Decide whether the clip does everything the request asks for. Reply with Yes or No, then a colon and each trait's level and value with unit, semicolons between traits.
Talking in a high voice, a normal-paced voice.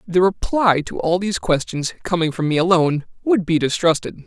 No: medium, 175 Hz; average, 185 wpm